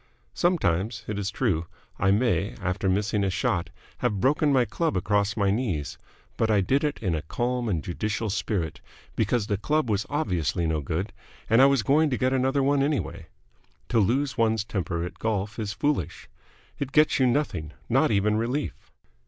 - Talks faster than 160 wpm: Yes, average, 180 wpm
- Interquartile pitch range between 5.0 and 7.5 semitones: Yes, wide, 5.5 semitones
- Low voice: Yes, low, 110 Hz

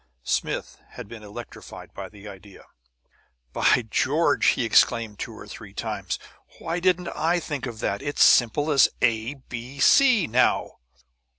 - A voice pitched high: No, low, 125 Hz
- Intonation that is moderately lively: No, wide, 5.7 semitones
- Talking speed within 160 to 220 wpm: No, average, 150 wpm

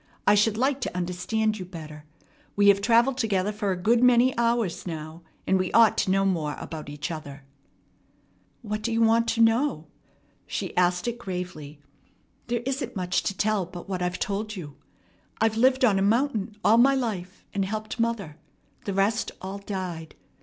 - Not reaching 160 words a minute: No, average, 180 wpm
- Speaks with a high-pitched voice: Yes, high, 205 Hz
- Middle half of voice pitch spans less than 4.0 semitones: No, average, 4.3 semitones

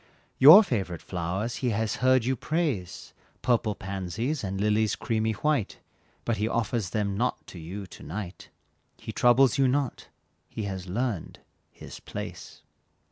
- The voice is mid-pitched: No, low, 110 Hz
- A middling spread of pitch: Yes, average, 4.5 semitones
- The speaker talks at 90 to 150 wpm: Yes, average, 145 wpm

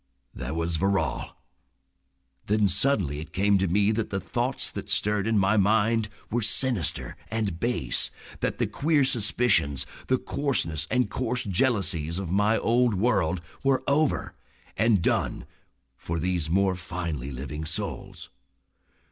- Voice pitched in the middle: No, low, 100 Hz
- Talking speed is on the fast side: No, average, 140 wpm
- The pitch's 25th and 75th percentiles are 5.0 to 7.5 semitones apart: Yes, average, 5.3 semitones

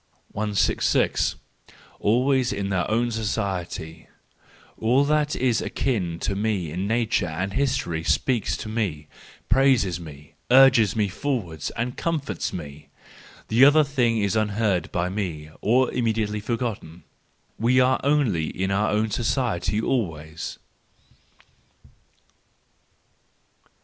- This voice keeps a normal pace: No, slow, 110 wpm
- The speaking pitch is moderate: No, low, 110 Hz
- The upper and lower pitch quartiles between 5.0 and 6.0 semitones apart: Yes, wide, 5.5 semitones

